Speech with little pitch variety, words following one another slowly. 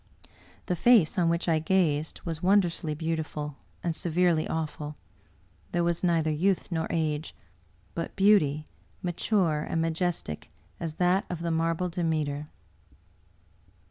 Yes: narrow, 2.2 semitones; slow, 125 wpm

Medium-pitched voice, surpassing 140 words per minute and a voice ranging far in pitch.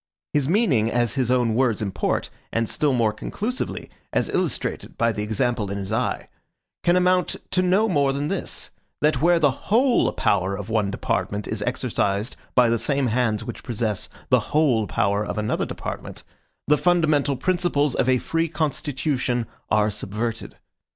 No: low, 125 Hz; average, 165 wpm; wide, 6.0 semitones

